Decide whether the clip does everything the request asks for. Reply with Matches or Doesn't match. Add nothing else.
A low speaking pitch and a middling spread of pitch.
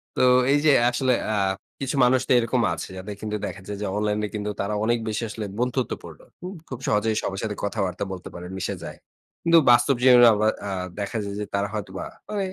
Matches